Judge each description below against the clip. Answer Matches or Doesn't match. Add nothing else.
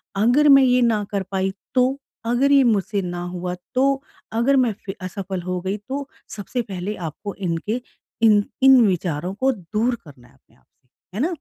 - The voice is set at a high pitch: Matches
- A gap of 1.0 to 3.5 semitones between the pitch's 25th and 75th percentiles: Doesn't match